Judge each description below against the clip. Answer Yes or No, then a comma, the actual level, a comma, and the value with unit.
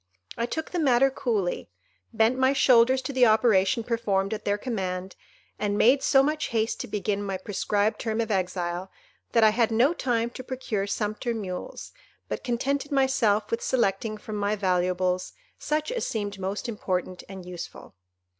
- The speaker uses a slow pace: No, average, 165 wpm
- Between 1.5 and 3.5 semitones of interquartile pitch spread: No, average, 4.5 semitones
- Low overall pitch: No, high, 220 Hz